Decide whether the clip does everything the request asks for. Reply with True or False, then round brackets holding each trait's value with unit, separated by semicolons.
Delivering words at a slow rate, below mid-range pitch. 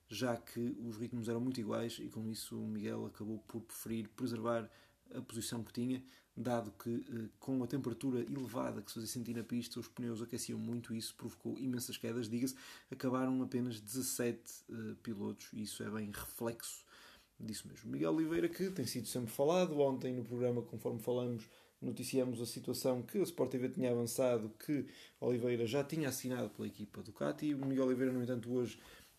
False (185 wpm; 120 Hz)